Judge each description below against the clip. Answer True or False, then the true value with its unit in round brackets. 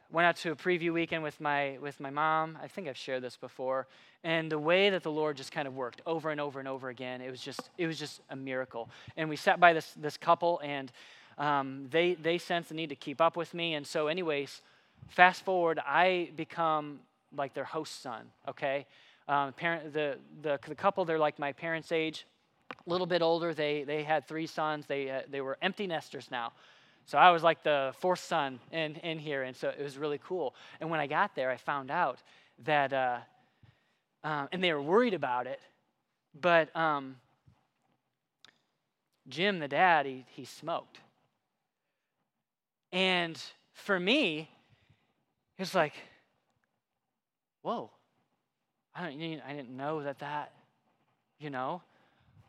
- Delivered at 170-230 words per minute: True (180 wpm)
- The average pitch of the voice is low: False (150 Hz)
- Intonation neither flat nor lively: True (3.2 semitones)